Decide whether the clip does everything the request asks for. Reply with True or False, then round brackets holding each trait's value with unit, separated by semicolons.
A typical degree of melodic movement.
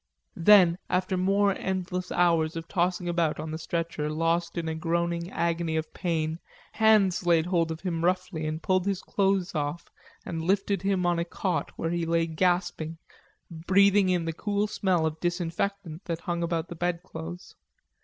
False (2.1 semitones)